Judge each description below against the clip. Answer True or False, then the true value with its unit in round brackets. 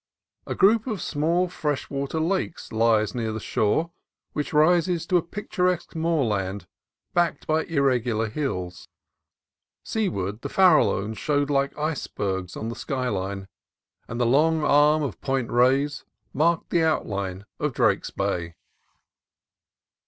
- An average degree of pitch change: False (6.8 semitones)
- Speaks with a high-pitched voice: False (140 Hz)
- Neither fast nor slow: False (130 wpm)